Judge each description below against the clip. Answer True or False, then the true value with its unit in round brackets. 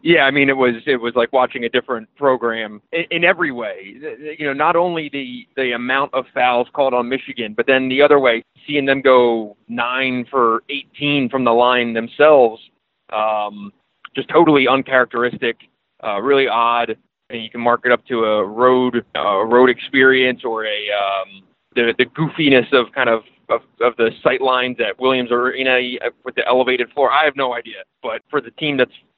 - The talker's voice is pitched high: False (125 Hz)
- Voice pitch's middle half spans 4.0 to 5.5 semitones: False (2.5 semitones)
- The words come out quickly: False (190 wpm)